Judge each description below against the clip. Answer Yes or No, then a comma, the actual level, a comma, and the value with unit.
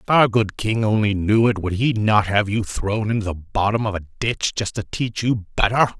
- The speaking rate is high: Yes, fast, 240 wpm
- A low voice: Yes, low, 105 Hz